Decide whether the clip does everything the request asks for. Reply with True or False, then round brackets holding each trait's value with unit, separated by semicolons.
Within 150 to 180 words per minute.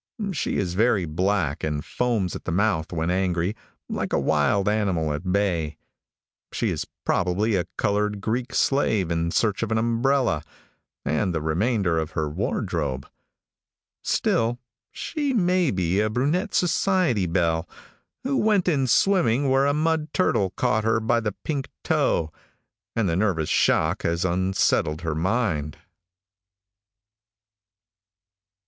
False (135 wpm)